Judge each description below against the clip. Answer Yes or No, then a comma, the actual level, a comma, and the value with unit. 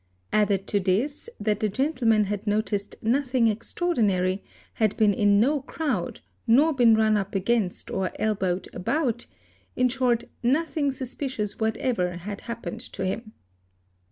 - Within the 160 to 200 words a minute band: No, average, 145 wpm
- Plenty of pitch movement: No, average, 4.0 semitones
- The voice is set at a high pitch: Yes, high, 220 Hz